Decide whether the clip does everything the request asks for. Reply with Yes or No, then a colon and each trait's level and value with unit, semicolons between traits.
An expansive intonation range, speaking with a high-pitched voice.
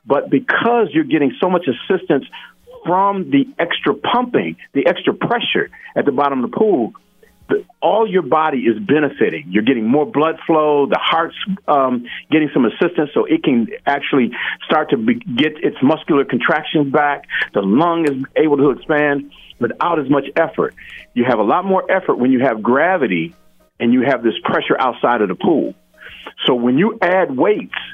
No: wide, 6.0 semitones; medium, 160 Hz